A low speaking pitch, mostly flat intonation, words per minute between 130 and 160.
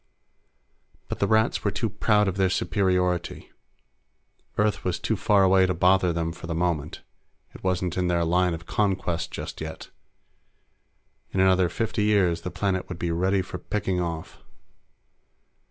Yes: very low, 90 Hz; narrow, 2.1 semitones; average, 155 wpm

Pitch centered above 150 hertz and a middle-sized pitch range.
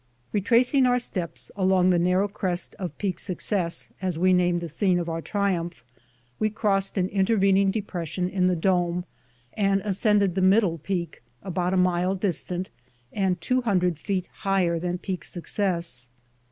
No: medium, 185 Hz; narrow, 2.1 semitones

